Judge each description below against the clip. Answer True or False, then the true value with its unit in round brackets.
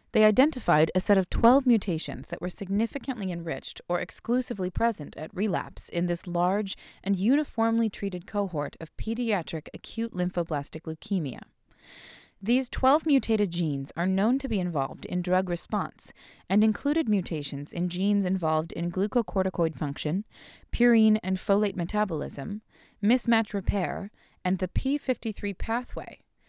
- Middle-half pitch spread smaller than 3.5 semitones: False (4.6 semitones)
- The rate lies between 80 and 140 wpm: True (135 wpm)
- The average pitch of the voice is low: False (195 Hz)